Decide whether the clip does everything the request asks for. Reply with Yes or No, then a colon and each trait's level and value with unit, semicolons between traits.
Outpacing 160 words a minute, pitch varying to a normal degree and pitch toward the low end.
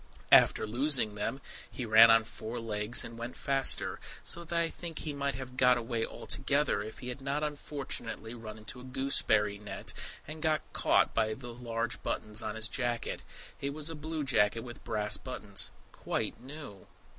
Yes: average, 180 wpm; average, 4.2 semitones; low, 120 Hz